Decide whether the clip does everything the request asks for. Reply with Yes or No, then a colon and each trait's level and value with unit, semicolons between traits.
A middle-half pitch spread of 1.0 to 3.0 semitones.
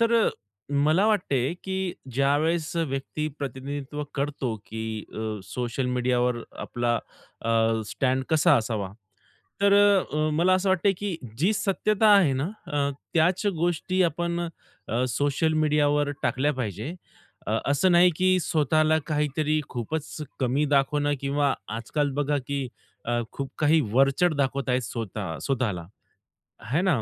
No: average, 4.5 semitones